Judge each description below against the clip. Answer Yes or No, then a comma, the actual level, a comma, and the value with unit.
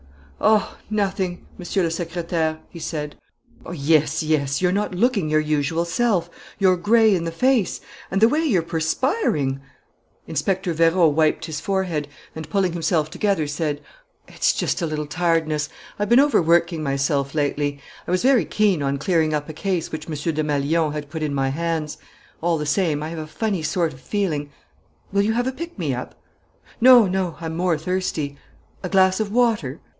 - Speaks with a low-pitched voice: No, medium, 165 Hz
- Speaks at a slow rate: No, average, 180 wpm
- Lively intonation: No, average, 4.0 semitones